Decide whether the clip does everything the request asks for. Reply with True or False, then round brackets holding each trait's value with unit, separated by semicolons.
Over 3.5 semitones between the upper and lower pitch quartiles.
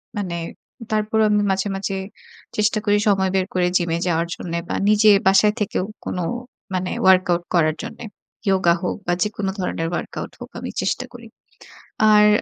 False (2.8 semitones)